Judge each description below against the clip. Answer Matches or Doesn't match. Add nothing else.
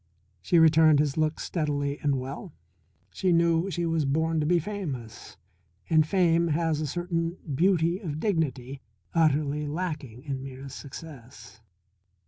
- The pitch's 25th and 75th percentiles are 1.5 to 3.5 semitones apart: Matches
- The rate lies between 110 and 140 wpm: Matches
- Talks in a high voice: Doesn't match